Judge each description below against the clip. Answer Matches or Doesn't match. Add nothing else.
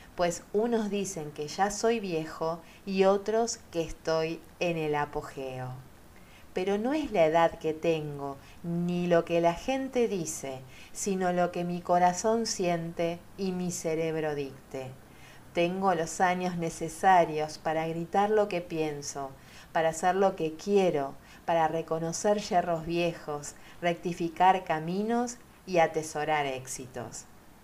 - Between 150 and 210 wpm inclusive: Doesn't match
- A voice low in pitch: Doesn't match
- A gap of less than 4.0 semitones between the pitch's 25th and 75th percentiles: Matches